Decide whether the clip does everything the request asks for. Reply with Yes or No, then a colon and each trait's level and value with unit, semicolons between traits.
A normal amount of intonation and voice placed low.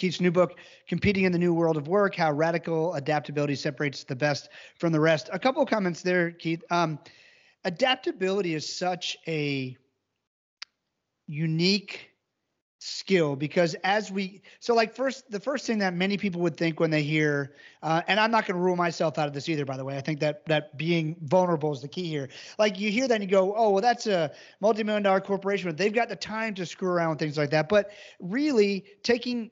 No: average, 4.6 semitones; medium, 180 Hz